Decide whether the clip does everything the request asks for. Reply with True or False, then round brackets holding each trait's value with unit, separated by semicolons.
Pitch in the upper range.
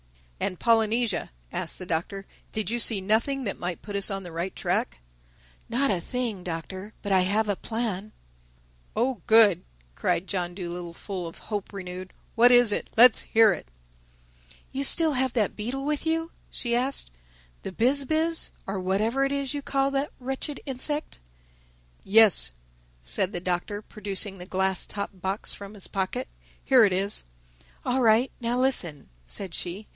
True (210 Hz)